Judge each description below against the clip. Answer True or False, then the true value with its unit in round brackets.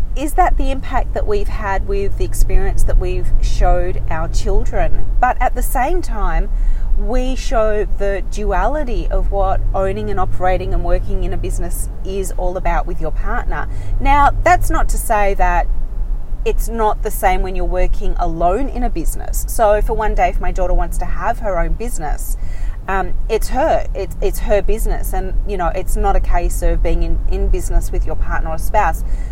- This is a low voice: False (175 Hz)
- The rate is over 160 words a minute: True (190 wpm)